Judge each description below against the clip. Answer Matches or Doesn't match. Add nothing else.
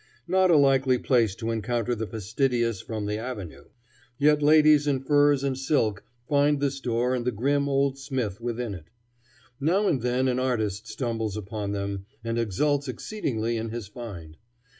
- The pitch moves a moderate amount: Matches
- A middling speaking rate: Matches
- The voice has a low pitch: Matches